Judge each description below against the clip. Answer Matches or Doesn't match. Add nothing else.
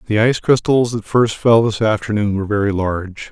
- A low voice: Matches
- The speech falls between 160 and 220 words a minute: Matches